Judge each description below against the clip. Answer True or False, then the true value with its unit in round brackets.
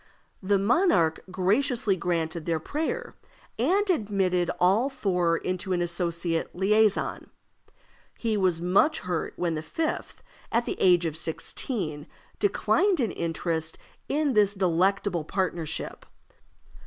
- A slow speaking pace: True (115 wpm)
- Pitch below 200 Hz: True (185 Hz)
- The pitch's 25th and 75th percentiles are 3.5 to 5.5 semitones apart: True (4.6 semitones)